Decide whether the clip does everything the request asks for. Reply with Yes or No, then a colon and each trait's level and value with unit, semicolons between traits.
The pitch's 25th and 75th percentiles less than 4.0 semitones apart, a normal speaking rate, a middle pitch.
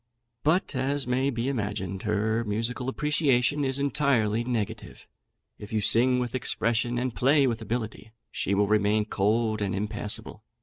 No: average, 3.6 semitones; average, 145 wpm; low, 115 Hz